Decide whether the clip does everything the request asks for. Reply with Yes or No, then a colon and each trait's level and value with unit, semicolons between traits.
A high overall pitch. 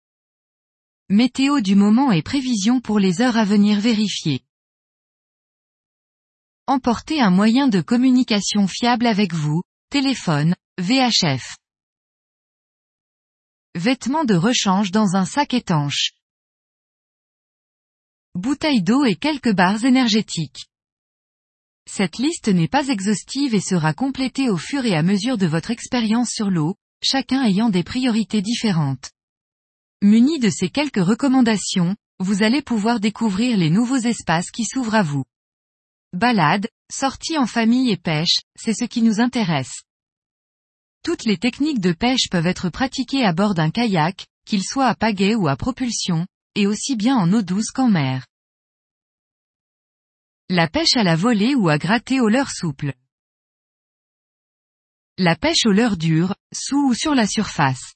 Yes: high, 215 Hz